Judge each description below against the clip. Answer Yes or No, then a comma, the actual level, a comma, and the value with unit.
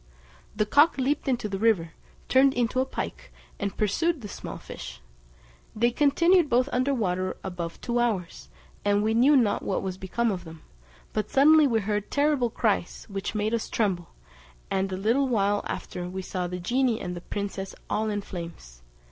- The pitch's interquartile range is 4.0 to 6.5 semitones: Yes, average, 5.1 semitones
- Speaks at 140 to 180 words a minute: Yes, average, 175 wpm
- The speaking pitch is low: No, high, 210 Hz